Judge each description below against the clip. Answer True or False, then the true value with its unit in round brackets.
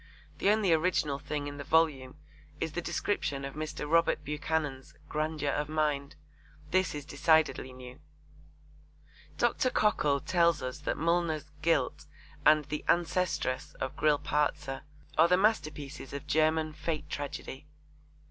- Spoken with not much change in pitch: True (2.3 semitones)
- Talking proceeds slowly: True (130 wpm)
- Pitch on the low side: False (150 Hz)